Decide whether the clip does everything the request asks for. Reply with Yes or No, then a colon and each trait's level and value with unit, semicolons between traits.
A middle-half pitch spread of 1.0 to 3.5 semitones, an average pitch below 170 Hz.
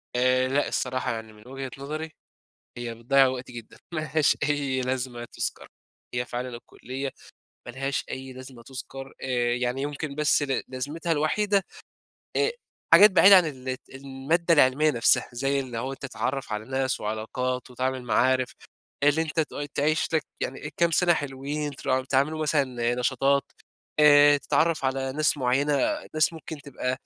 Yes: average, 2.7 semitones; low, 135 Hz